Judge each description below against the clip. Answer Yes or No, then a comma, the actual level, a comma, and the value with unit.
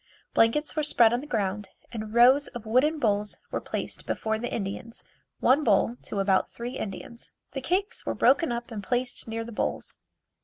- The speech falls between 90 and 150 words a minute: No, average, 185 wpm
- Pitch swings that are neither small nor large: Yes, average, 3.4 semitones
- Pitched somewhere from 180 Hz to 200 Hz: No, high, 235 Hz